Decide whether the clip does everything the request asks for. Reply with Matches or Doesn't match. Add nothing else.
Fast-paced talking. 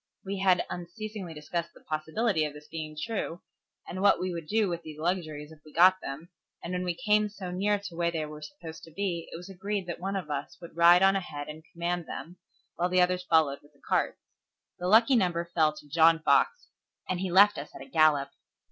Matches